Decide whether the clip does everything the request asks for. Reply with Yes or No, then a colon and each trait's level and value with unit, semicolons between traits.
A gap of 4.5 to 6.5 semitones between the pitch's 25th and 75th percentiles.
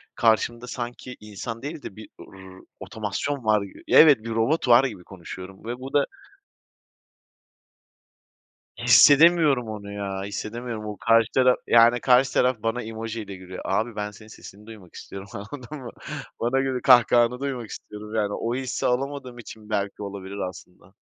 No: average, 3.5 semitones